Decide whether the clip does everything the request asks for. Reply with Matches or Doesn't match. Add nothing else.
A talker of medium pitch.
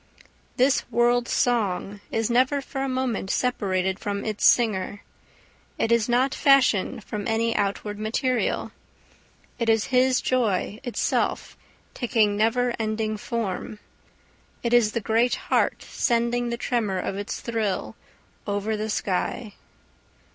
Doesn't match